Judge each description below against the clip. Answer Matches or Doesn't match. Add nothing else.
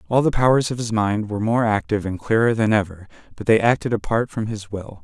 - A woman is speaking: Doesn't match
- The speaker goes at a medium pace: Doesn't match